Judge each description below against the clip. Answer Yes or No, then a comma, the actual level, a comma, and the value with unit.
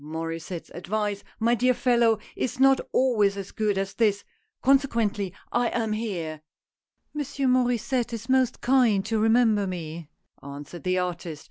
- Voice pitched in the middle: No, high, 215 Hz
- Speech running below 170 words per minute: Yes, average, 160 wpm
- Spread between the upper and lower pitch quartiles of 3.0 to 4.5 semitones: No, average, 5.0 semitones